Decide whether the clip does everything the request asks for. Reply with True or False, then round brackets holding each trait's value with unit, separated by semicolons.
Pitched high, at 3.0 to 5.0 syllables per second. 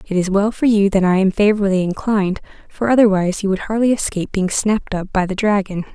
False (200 Hz; 6.4 syllables/s)